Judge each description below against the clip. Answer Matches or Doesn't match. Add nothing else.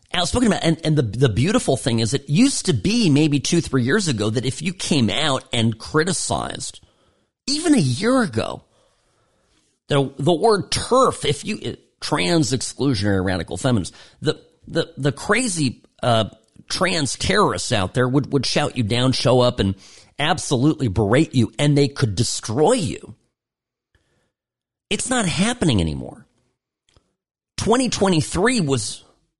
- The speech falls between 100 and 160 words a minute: Matches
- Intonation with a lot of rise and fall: Matches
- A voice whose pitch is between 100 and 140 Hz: Matches